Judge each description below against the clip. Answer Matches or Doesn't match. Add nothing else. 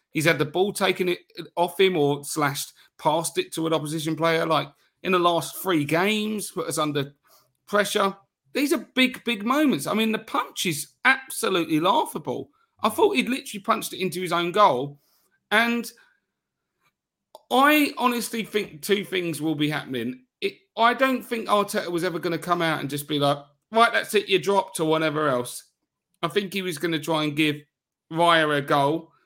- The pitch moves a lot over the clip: Matches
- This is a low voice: Doesn't match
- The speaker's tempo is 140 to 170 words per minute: Doesn't match